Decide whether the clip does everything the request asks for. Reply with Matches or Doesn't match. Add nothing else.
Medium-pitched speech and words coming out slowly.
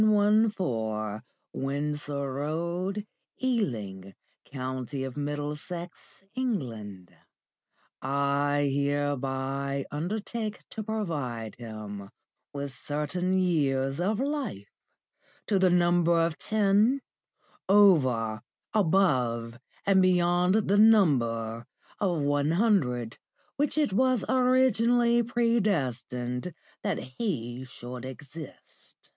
Matches